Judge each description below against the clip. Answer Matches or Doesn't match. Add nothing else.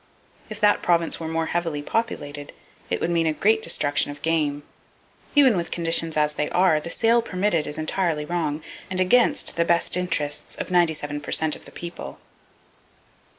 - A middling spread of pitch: Matches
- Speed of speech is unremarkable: Matches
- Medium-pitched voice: Matches